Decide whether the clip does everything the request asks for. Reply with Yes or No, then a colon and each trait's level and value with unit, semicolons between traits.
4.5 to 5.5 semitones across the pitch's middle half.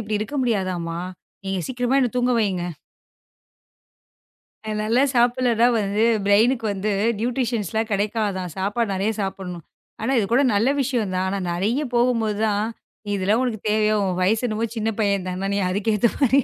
No: average, 3.3 semitones